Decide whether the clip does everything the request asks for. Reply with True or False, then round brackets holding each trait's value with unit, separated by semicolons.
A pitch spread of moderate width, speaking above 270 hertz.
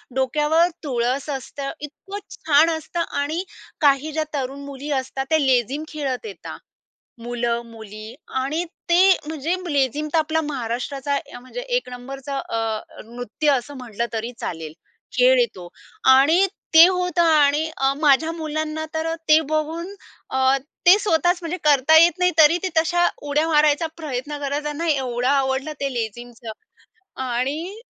True (3.6 semitones; 290 Hz)